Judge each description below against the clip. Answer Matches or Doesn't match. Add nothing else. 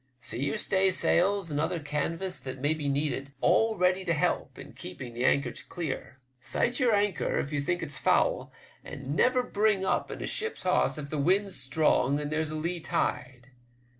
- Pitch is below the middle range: Doesn't match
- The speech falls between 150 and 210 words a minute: Matches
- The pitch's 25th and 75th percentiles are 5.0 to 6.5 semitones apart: Matches